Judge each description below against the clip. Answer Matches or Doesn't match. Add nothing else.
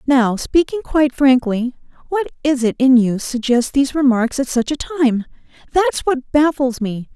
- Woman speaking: Matches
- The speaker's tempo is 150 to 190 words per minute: Matches